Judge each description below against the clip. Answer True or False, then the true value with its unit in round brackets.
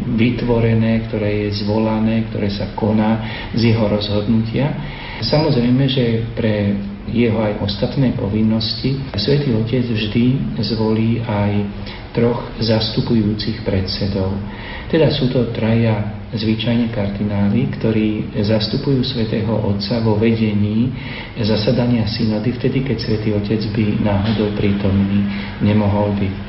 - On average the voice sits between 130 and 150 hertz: False (110 Hz)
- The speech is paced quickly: False (110 wpm)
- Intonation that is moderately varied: False (2.1 semitones)